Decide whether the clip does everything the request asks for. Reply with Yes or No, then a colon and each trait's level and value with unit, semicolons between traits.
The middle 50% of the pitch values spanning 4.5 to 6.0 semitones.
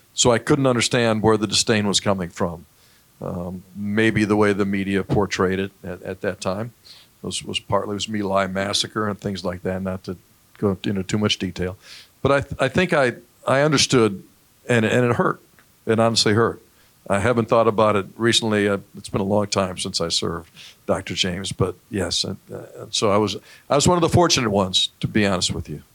No: average, 2.8 semitones